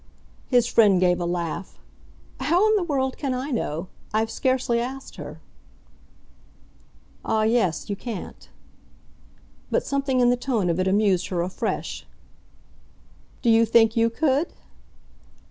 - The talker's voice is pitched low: No, high, 230 Hz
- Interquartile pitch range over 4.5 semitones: Yes, wide, 5.5 semitones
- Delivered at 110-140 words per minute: Yes, slow, 135 wpm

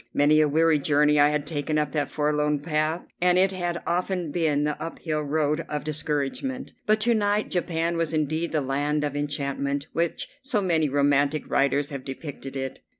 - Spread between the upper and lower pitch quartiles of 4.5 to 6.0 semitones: No, narrow, 2.6 semitones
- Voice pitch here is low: No, medium, 150 Hz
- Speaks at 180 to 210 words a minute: Yes, average, 185 wpm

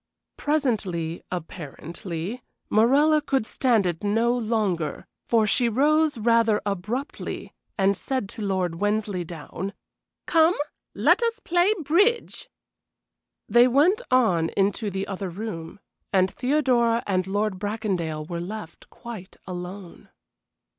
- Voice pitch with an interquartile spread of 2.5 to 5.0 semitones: No, wide, 5.5 semitones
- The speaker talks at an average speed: No, slow, 115 wpm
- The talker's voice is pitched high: Yes, high, 210 Hz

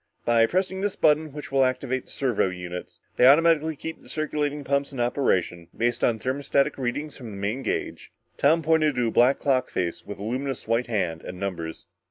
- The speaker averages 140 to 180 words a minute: No, average, 200 wpm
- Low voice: Yes, low, 130 Hz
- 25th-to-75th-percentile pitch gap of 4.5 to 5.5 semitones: Yes, average, 5.0 semitones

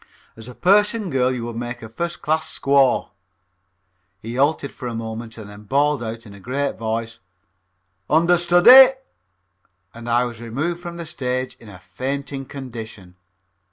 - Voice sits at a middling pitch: No, low, 125 Hz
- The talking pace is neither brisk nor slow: Yes, average, 155 wpm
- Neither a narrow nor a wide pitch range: Yes, average, 4.7 semitones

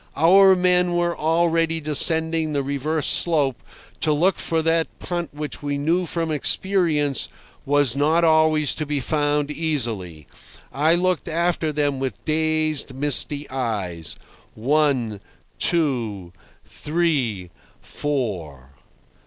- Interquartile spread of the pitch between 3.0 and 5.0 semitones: Yes, average, 3.3 semitones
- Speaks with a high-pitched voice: No, medium, 150 Hz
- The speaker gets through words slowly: Yes, slow, 115 wpm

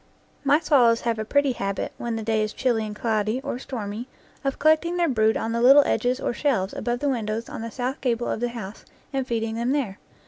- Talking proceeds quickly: Yes, fast, 235 wpm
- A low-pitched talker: No, high, 235 Hz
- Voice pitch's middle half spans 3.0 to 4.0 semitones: Yes, average, 3.3 semitones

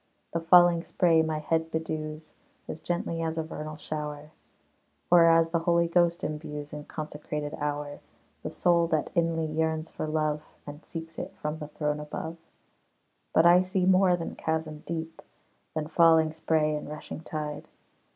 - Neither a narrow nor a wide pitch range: No, narrow, 1.6 semitones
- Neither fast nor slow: Yes, average, 160 wpm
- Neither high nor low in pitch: Yes, medium, 160 Hz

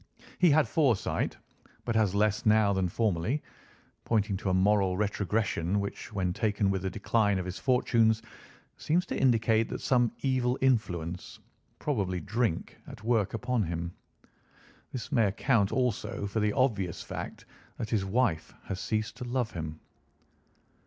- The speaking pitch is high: No, low, 105 Hz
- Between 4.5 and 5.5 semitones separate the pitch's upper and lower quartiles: No, average, 4.0 semitones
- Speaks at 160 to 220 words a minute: No, average, 145 wpm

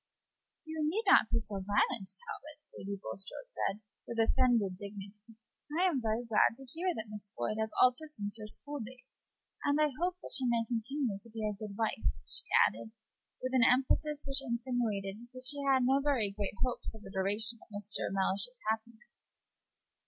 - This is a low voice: No, high, 230 Hz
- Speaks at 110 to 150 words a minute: No, average, 180 wpm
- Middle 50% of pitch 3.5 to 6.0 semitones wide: Yes, average, 4.6 semitones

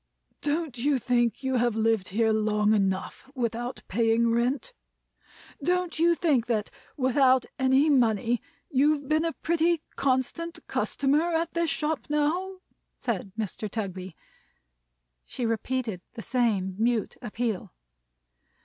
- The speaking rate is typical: No, slow, 125 wpm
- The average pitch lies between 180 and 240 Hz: No, very high, 250 Hz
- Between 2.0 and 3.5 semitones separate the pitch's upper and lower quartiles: No, average, 5.0 semitones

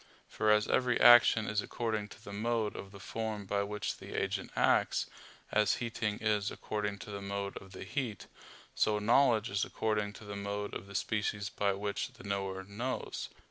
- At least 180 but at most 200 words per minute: Yes, average, 185 wpm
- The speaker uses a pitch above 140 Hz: No, low, 105 Hz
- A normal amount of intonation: No, narrow, 1.7 semitones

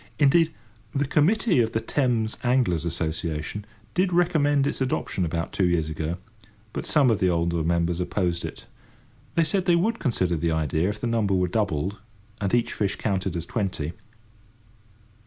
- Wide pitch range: Yes, wide, 8.3 semitones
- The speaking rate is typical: Yes, average, 165 wpm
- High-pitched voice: No, low, 100 Hz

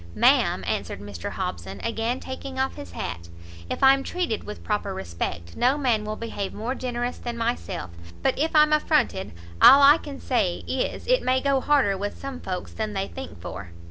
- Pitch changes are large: Yes, wide, 6.0 semitones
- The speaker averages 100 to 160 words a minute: No, average, 185 wpm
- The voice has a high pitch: Yes, high, 235 Hz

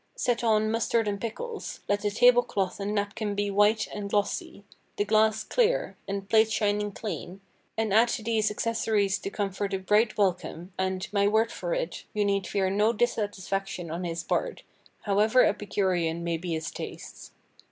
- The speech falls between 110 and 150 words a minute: No, average, 175 wpm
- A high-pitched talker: Yes, high, 205 Hz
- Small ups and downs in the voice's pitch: Yes, narrow, 2.1 semitones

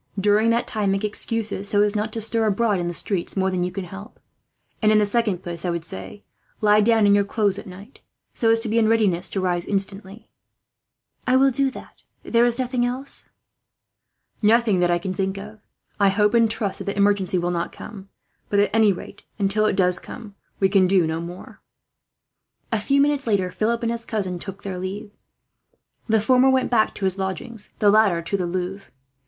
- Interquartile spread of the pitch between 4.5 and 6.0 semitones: No, average, 3.0 semitones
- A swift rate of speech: Yes, fast, 215 wpm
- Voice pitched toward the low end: No, high, 205 Hz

